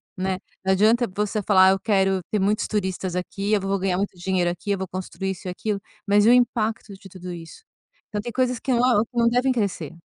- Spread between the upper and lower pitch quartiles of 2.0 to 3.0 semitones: Yes, average, 2.7 semitones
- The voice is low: No, high, 200 Hz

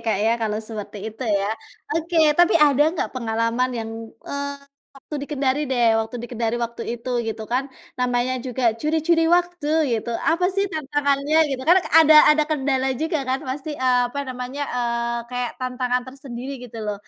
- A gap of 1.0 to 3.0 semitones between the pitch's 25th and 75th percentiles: No, average, 3.7 semitones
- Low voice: No, very high, 255 Hz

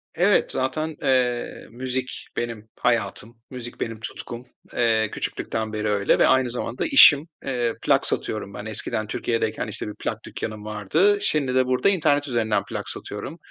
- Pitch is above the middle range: No, low, 120 Hz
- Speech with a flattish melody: No, average, 3.1 semitones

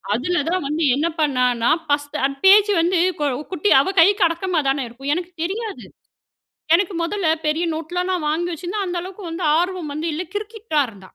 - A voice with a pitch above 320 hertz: Yes, very high, 345 Hz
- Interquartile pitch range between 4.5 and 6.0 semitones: No, average, 4.1 semitones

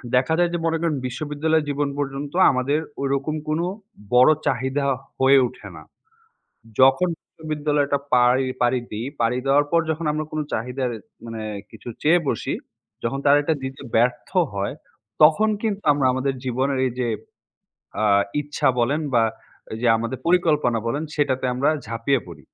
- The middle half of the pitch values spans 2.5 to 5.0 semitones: Yes, average, 3.4 semitones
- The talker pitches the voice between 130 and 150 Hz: Yes, low, 135 Hz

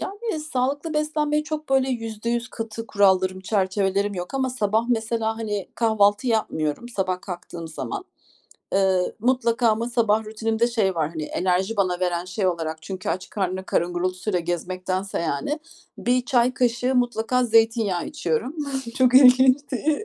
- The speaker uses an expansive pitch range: No, average, 5.0 semitones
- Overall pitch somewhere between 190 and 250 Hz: Yes, high, 220 Hz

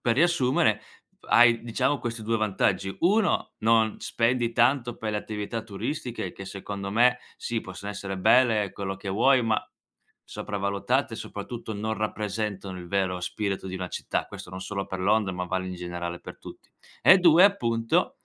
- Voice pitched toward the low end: Yes, low, 110 Hz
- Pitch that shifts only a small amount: No, average, 3.5 semitones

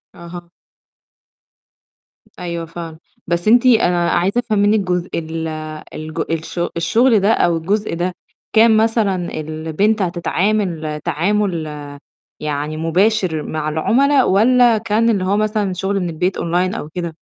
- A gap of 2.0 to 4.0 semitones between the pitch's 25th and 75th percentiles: No, average, 4.4 semitones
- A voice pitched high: No, medium, 180 Hz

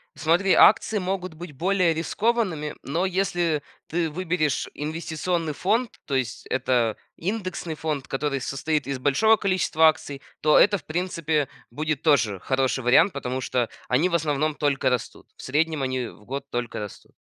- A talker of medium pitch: Yes, medium, 155 Hz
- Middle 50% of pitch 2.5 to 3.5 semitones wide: No, average, 4.8 semitones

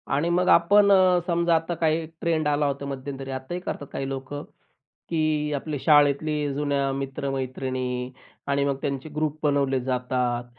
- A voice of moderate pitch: Yes, medium, 145 Hz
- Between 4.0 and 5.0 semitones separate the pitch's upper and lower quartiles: No, average, 2.7 semitones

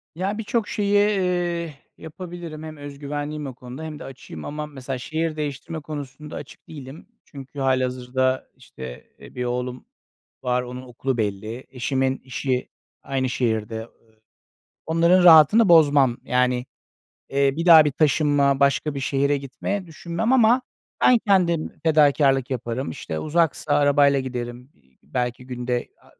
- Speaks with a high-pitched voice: No, medium, 140 Hz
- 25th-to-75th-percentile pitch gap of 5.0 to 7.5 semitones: No, average, 3.9 semitones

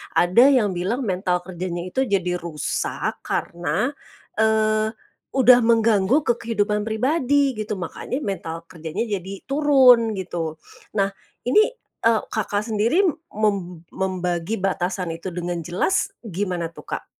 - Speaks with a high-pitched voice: Yes, high, 200 Hz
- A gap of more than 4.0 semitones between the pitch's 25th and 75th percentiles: Yes, average, 4.6 semitones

